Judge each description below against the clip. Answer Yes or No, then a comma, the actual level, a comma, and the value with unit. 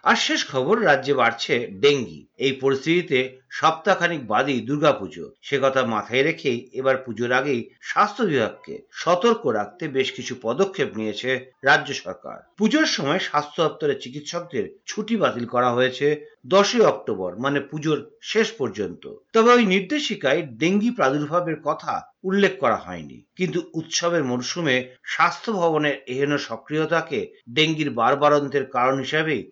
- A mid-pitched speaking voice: Yes, medium, 155 Hz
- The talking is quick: Yes, fast, 130 wpm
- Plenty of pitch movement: Yes, wide, 6.3 semitones